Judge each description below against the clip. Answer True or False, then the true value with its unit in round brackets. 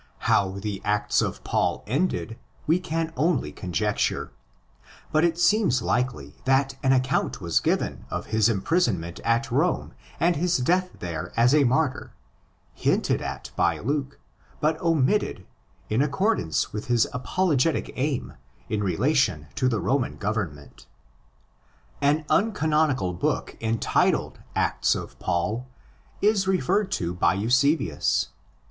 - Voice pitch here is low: True (130 Hz)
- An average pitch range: False (7.3 semitones)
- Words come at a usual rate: False (130 wpm)